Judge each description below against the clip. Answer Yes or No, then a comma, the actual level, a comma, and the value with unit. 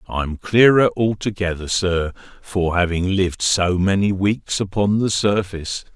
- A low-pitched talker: Yes, very low, 95 Hz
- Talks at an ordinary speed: No, slow, 130 wpm